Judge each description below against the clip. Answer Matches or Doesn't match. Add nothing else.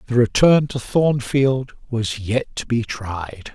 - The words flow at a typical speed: Matches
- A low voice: Matches